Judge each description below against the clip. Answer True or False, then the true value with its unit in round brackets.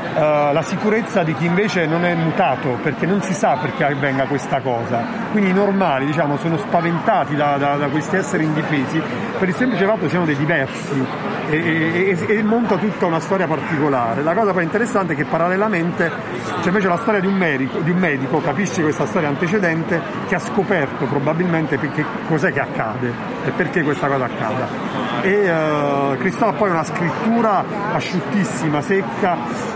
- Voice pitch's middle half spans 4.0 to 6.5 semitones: True (4.5 semitones)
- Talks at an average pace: False (175 wpm)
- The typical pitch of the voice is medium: True (170 Hz)